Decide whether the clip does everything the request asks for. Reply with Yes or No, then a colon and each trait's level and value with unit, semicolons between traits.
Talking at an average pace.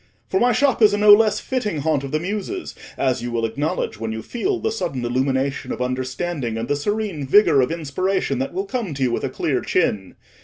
No: fast, 225 wpm